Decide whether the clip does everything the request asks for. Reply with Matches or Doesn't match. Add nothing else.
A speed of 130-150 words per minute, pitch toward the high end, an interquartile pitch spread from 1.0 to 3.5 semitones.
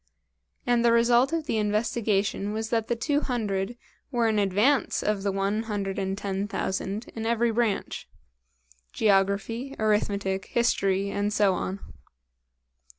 Matches